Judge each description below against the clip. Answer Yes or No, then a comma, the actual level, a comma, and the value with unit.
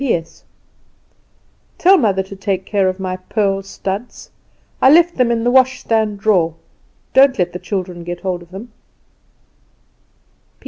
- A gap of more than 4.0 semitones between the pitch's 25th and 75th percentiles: Yes, average, 4.4 semitones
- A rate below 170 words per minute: Yes, average, 150 wpm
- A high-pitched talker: Yes, high, 195 Hz